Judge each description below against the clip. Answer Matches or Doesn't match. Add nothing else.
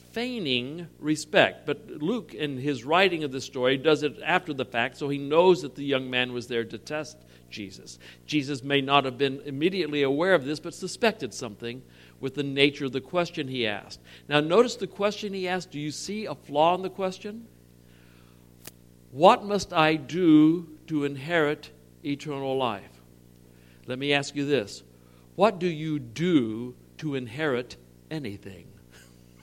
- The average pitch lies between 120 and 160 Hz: Matches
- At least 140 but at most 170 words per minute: Matches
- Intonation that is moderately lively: Doesn't match